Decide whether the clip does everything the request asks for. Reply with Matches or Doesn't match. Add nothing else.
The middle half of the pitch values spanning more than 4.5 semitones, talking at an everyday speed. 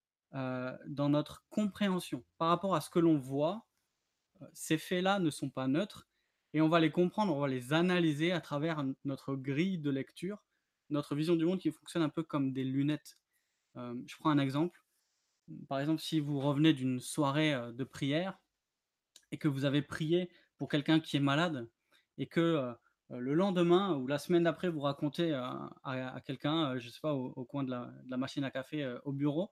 Doesn't match